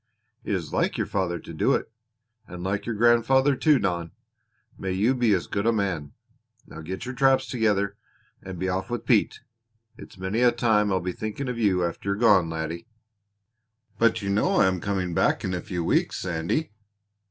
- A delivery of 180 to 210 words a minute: Yes, average, 200 wpm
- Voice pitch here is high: No, low, 100 Hz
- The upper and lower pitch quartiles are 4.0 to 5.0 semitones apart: Yes, average, 4.4 semitones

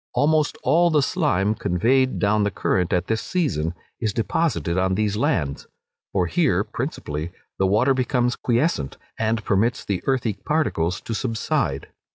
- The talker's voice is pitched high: No, low, 110 Hz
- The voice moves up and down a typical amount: No, wide, 6.0 semitones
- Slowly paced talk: No, average, 150 wpm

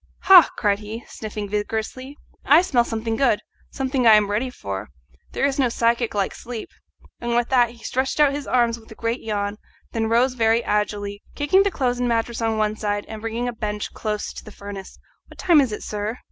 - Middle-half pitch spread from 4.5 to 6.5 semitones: No, average, 3.0 semitones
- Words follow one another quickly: Yes, fast, 210 wpm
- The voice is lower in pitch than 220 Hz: No, high, 230 Hz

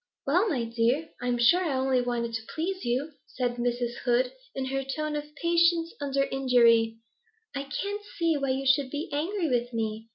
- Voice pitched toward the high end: Yes, very high, 270 Hz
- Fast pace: No, average, 185 wpm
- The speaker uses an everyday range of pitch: Yes, average, 4.2 semitones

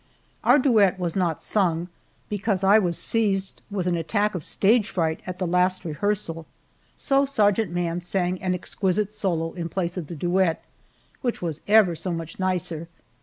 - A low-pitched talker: No, medium, 185 Hz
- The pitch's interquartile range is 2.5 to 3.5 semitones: Yes, average, 3.2 semitones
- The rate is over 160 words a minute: Yes, average, 170 wpm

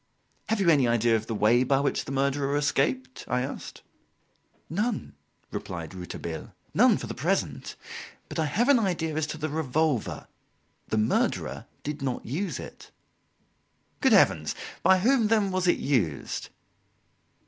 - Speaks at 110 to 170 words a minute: Yes, average, 150 wpm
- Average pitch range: No, wide, 5.9 semitones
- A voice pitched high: No, medium, 145 Hz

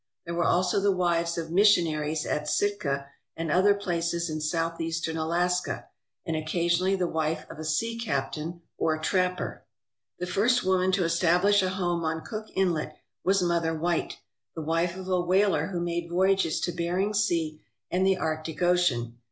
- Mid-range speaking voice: Yes, medium, 170 Hz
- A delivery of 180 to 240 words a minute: No, average, 170 wpm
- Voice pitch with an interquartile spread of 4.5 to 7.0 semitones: No, narrow, 2.4 semitones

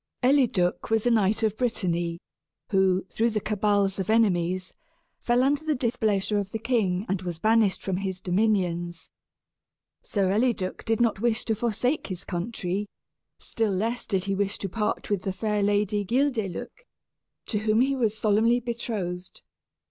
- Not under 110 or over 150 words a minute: No, average, 160 wpm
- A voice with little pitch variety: No, average, 3.3 semitones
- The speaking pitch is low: No, high, 210 Hz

